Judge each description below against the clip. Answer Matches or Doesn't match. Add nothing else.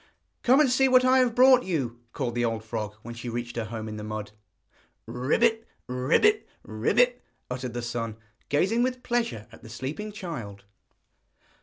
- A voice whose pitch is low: Matches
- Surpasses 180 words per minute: Doesn't match